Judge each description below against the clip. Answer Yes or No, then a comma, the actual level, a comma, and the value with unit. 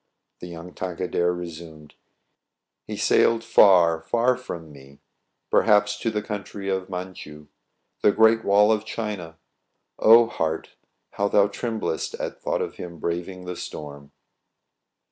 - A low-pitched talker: Yes, very low, 90 Hz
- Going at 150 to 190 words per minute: No, average, 140 wpm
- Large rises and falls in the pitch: No, average, 4.2 semitones